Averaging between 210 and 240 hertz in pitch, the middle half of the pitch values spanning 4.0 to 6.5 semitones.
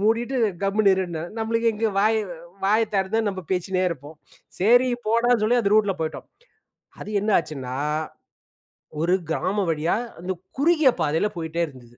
No: high, 195 Hz; average, 5.2 semitones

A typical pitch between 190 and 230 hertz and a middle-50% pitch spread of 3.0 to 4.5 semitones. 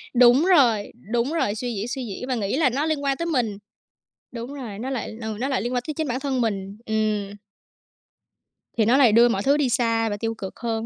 No: high, 240 Hz; average, 3.6 semitones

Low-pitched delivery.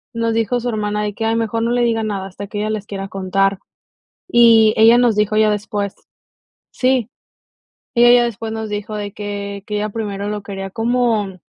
No: high, 215 Hz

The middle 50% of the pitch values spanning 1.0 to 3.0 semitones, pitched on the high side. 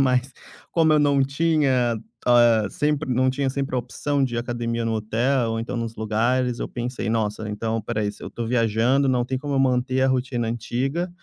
No: average, 2.7 semitones; low, 125 Hz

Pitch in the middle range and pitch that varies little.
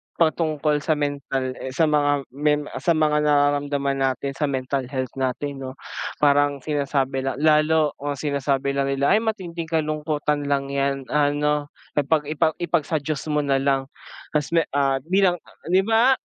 Yes: medium, 145 Hz; narrow, 1.9 semitones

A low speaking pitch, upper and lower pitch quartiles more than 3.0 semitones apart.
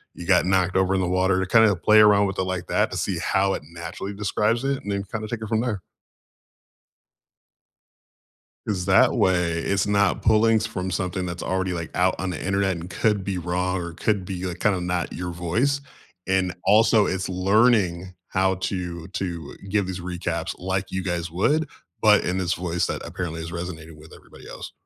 No: very low, 95 Hz; narrow, 2.5 semitones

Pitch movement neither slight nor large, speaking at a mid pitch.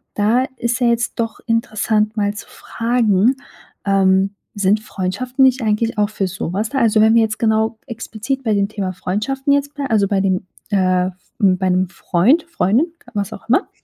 No: average, 3.2 semitones; high, 215 Hz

